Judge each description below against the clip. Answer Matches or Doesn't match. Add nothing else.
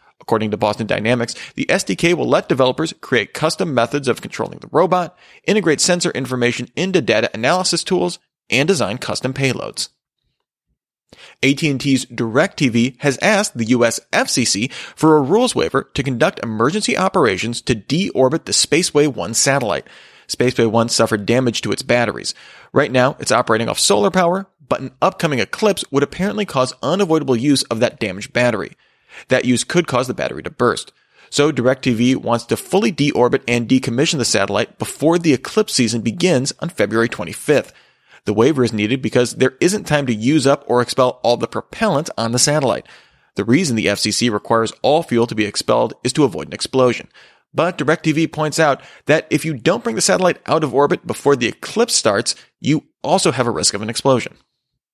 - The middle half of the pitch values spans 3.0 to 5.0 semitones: Doesn't match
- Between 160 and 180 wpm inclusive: Matches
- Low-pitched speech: Matches